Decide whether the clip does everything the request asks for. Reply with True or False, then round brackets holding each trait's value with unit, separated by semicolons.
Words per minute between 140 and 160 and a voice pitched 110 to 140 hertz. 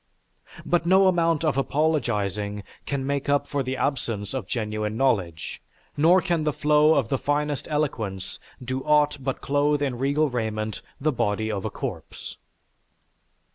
True (150 wpm; 135 Hz)